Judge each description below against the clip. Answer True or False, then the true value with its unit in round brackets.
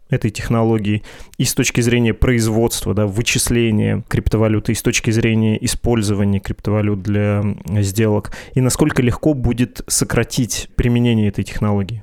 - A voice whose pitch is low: True (115 Hz)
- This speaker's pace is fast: False (130 wpm)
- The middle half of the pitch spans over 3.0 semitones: False (2.6 semitones)